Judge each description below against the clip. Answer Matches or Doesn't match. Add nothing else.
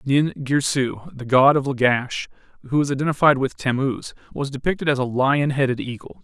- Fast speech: Doesn't match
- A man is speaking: Matches